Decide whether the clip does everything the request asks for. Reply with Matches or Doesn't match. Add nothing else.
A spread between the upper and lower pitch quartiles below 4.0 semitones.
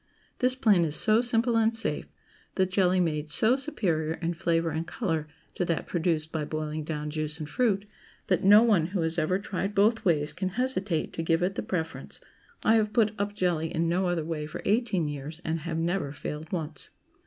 Doesn't match